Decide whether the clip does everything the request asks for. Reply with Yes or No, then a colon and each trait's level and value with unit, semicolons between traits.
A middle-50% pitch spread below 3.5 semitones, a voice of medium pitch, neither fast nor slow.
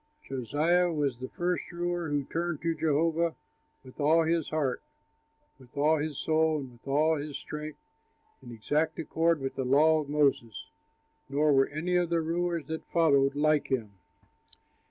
Yes: average, 2.9 semitones; medium, 155 Hz; average, 160 wpm